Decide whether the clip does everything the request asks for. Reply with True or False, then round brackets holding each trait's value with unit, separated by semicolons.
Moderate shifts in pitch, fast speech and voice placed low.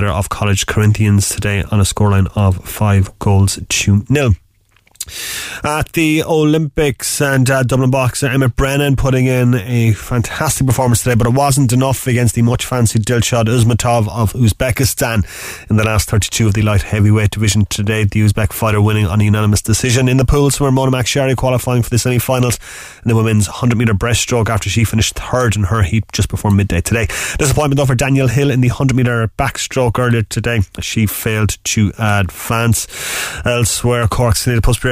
False (3.5 semitones; 185 wpm; 115 Hz)